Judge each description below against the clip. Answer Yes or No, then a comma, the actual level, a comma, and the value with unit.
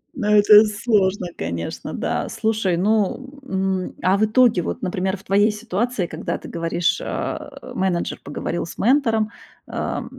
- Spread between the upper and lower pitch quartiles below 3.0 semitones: No, average, 3.3 semitones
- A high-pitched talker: Yes, high, 205 Hz